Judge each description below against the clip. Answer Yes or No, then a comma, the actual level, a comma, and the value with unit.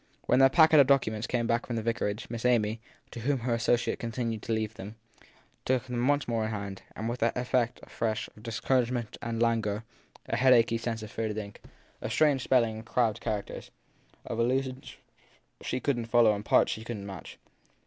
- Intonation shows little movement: Yes, narrow, 2.1 semitones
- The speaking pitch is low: Yes, low, 115 Hz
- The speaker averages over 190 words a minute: Yes, average, 200 wpm